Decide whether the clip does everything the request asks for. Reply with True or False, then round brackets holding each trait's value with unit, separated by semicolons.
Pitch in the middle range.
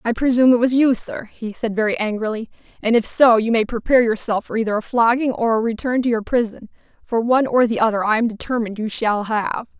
False (230 Hz)